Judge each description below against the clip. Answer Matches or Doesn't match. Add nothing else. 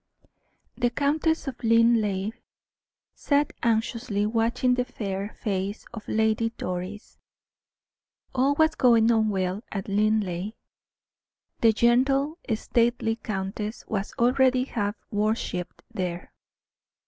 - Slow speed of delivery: Matches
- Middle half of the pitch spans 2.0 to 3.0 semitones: Doesn't match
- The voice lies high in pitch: Matches